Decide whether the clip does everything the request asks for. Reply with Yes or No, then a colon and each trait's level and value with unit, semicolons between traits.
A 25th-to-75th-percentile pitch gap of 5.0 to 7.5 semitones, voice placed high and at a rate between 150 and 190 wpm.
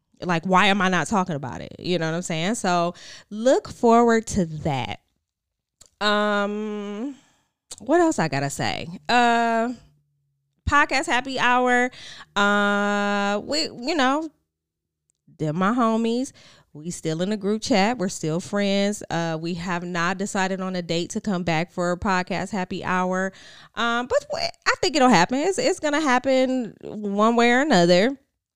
Yes: wide, 5.6 semitones; high, 200 Hz; average, 160 wpm